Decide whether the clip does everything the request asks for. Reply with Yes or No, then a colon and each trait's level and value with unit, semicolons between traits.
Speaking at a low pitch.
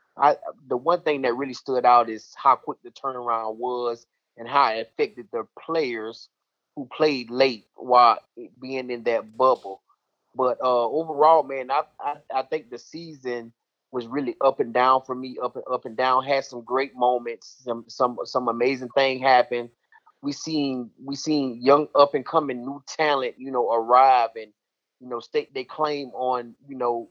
Yes: low, 130 Hz